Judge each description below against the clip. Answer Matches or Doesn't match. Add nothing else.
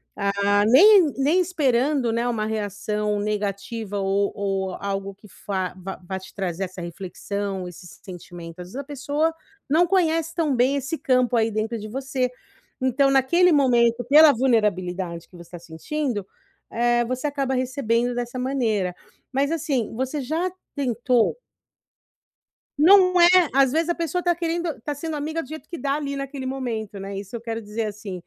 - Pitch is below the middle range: Doesn't match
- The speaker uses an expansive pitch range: Matches